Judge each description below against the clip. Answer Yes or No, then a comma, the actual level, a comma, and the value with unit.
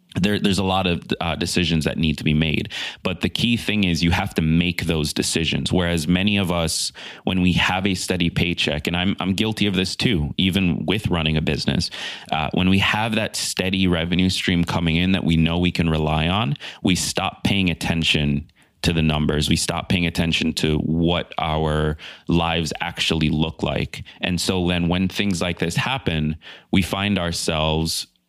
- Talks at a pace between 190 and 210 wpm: Yes, average, 195 wpm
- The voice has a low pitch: Yes, very low, 85 Hz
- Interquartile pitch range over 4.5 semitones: No, average, 2.8 semitones